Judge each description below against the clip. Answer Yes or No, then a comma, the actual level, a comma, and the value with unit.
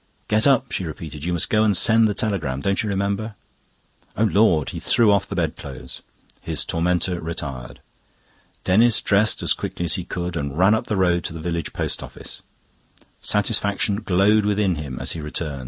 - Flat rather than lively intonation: No, average, 4.3 semitones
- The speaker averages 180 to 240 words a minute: Yes, average, 190 wpm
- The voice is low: Yes, very low, 95 Hz